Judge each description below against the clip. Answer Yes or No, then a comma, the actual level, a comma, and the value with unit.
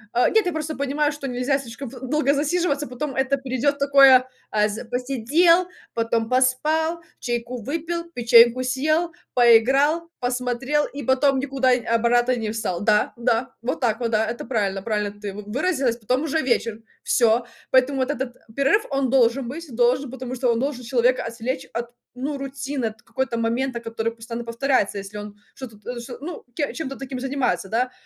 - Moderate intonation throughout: Yes, average, 3.1 semitones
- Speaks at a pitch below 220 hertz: No, very high, 255 Hz